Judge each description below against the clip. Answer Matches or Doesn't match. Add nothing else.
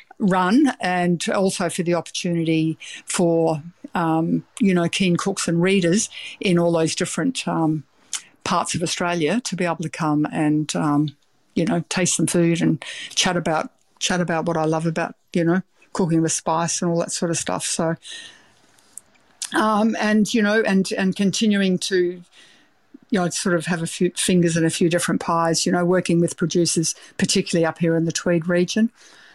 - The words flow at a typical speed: Matches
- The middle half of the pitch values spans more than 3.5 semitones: Doesn't match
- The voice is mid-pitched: Matches